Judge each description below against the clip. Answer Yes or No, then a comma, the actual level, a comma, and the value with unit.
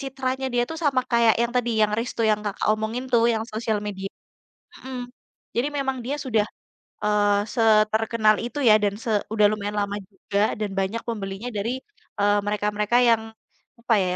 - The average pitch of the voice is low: No, high, 220 Hz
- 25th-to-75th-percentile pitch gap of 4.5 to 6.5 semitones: No, average, 2.7 semitones